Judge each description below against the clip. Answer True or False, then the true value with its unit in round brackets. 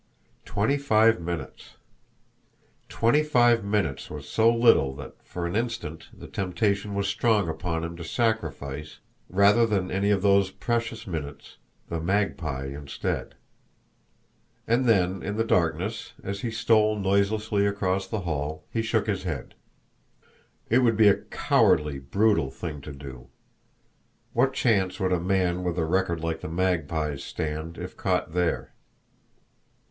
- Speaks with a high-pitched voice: False (95 Hz)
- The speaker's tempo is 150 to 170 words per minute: False (140 wpm)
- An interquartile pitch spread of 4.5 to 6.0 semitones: True (5.1 semitones)